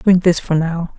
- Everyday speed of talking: No, fast, 245 wpm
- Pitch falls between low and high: Yes, medium, 175 Hz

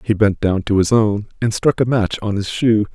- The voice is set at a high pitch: No, low, 105 Hz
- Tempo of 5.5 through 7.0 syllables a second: No, 5.0 syllables/s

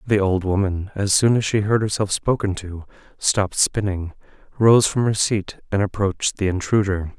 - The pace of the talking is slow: No, average, 175 wpm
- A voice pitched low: Yes, low, 100 Hz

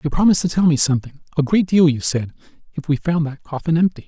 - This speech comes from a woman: No, male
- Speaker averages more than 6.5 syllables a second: Yes, 6.8 syllables/s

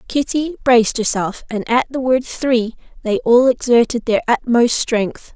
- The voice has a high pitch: Yes, high, 240 Hz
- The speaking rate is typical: Yes, average, 155 wpm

